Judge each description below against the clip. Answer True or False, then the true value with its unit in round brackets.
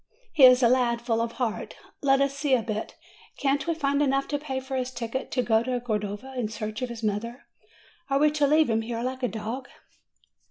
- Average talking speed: False (225 wpm)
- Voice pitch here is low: False (250 Hz)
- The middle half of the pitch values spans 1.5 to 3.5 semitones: True (3.1 semitones)